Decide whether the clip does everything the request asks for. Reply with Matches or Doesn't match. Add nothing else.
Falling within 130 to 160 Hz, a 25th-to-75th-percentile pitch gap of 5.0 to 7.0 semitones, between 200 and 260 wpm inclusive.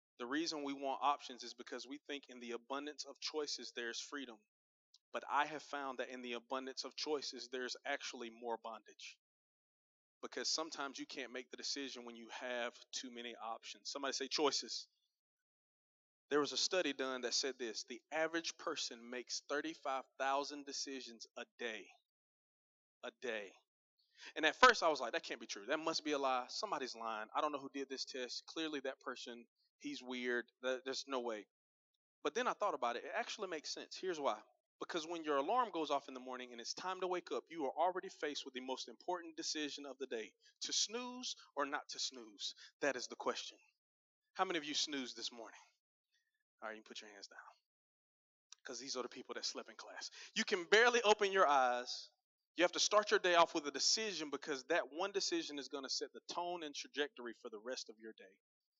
Matches